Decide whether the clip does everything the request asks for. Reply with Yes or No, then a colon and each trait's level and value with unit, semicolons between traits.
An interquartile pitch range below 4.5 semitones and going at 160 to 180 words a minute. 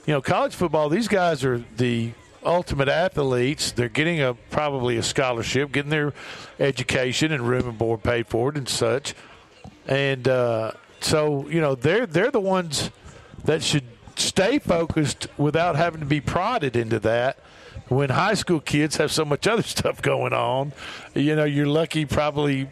Yes: average, 3.9 semitones; average, 170 wpm